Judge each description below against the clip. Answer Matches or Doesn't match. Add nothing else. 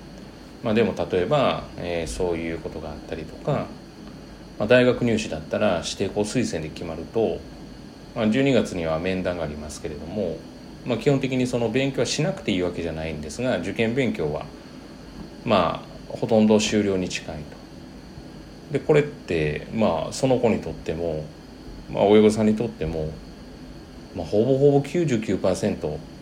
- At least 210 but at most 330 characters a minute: Matches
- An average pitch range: Doesn't match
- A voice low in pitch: Matches